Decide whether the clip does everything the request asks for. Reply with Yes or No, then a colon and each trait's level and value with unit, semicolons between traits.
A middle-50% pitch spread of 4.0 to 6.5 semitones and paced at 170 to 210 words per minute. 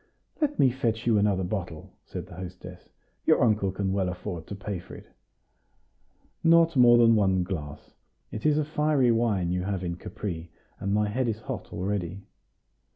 Yes: average, 4.6 semitones; average, 175 wpm